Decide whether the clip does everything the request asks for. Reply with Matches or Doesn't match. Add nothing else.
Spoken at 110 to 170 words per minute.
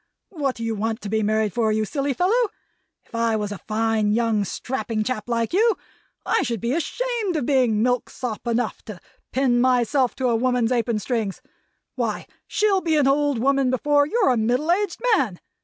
Doesn't match